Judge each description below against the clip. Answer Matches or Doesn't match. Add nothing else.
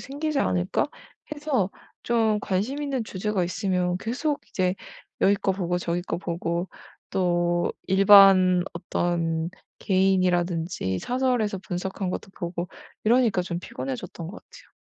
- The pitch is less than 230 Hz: Matches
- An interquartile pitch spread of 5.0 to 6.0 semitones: Doesn't match